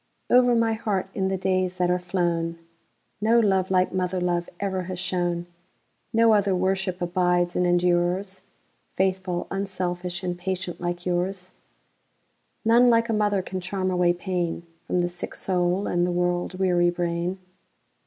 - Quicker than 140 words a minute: No, slow, 135 wpm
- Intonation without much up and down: Yes, narrow, 1.5 semitones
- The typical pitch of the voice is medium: Yes, medium, 180 Hz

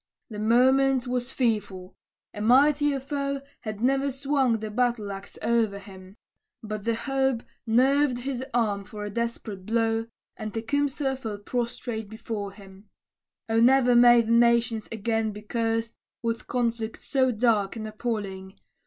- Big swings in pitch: No, average, 3.0 semitones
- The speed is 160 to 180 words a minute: No, average, 140 wpm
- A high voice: Yes, high, 230 Hz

